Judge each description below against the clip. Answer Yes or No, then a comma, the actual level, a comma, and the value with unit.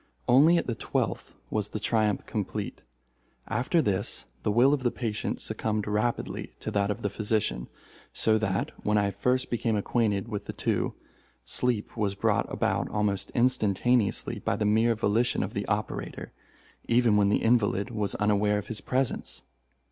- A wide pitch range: No, average, 2.7 semitones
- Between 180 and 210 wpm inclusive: No, average, 165 wpm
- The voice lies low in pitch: Yes, low, 110 Hz